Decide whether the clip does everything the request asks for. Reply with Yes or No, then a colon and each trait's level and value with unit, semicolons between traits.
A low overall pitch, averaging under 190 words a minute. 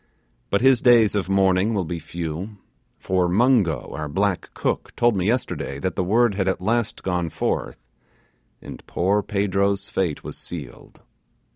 Yes: very low, 95 Hz; average, 155 wpm